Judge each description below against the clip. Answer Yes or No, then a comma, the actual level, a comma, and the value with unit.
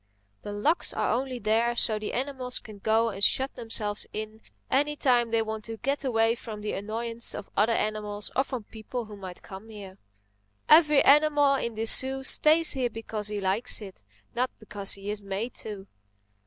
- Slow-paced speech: No, average, 185 wpm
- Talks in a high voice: Yes, high, 225 Hz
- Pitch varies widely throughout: No, average, 3.5 semitones